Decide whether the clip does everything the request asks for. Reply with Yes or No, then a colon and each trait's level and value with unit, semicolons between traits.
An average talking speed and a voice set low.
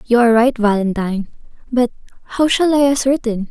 No: average, 155 wpm; high, 240 Hz